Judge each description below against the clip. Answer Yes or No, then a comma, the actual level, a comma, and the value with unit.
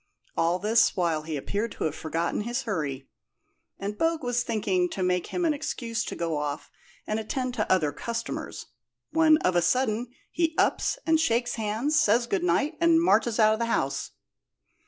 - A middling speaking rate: Yes, average, 180 wpm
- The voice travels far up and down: Yes, wide, 5.9 semitones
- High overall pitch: Yes, high, 220 Hz